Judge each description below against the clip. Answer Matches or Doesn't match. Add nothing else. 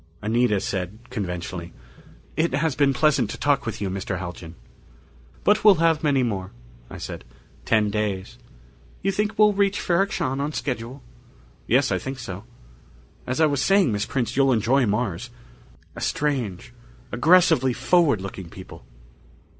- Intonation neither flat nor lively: Doesn't match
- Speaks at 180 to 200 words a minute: Doesn't match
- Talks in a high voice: Doesn't match